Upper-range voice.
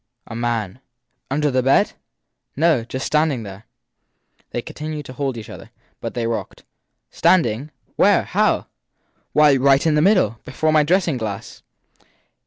No: low, 135 Hz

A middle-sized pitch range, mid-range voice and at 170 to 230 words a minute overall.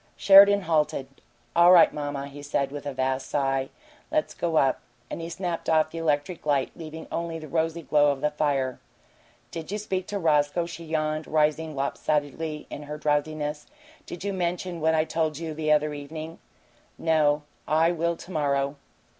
No: narrow, 2.3 semitones; medium, 155 Hz; average, 180 wpm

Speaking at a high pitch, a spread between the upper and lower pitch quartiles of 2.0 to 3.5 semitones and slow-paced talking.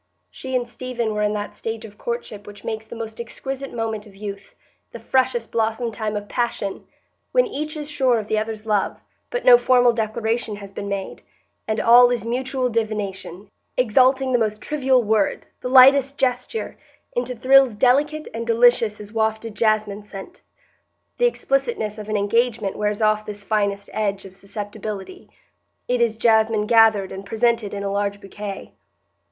No: high, 225 Hz; average, 3.0 semitones; average, 165 wpm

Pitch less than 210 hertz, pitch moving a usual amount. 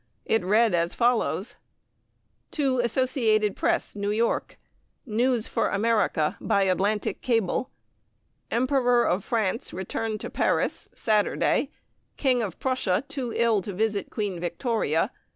No: high, 220 Hz; average, 3.5 semitones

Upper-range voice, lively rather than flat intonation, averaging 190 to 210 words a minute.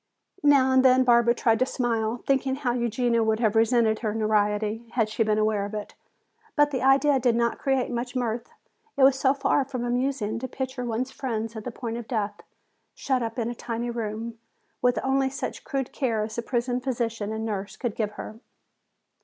No: high, 235 Hz; average, 2.8 semitones; average, 200 wpm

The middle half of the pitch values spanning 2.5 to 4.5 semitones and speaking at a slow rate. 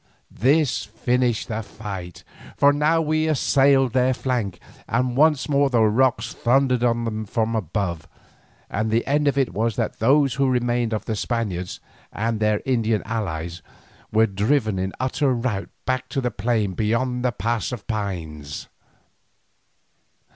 No: average, 3.5 semitones; average, 150 wpm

